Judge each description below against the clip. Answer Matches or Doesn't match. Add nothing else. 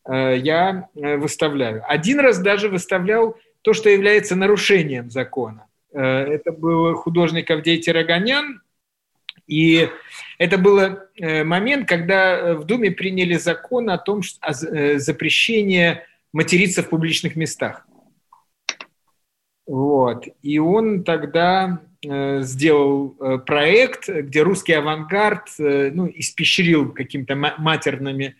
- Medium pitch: Matches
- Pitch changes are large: Doesn't match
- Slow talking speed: Matches